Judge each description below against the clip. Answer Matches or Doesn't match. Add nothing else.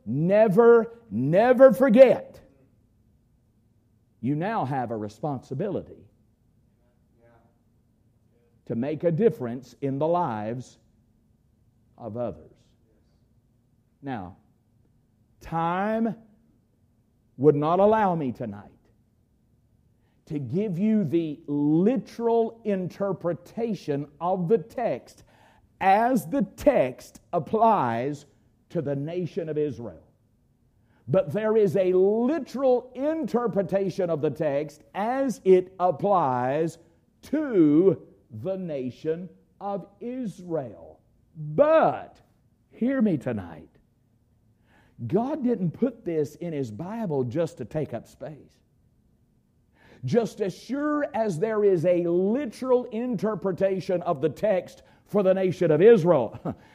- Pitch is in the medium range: Matches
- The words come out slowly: Matches